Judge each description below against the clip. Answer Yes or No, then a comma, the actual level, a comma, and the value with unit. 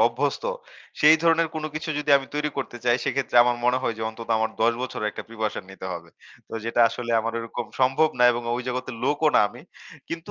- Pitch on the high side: No, low, 125 Hz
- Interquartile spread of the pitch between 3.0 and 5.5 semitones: Yes, average, 4.5 semitones